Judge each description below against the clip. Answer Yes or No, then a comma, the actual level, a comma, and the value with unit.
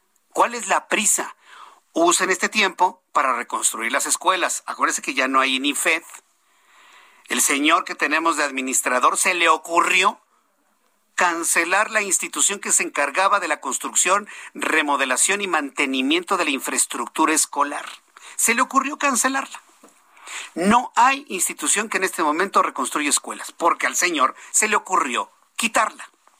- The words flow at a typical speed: Yes, average, 145 wpm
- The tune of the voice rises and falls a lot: Yes, wide, 6.6 semitones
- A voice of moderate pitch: Yes, medium, 180 Hz